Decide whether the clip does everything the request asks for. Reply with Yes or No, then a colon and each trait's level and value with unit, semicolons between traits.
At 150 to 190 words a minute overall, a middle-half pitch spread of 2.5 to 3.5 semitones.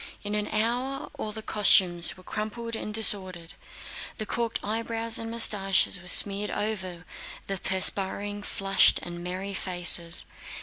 No: slow, 135 wpm; average, 2.9 semitones